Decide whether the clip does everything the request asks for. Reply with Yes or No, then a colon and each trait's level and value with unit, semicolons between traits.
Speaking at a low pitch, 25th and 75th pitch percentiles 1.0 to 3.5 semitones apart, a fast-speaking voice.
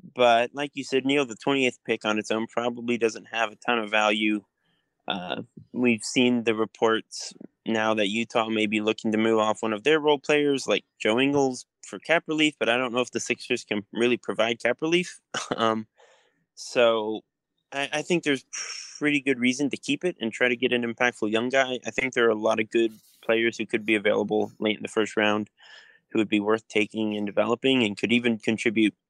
Yes: low, 115 Hz; average, 2.9 semitones; fast, 215 wpm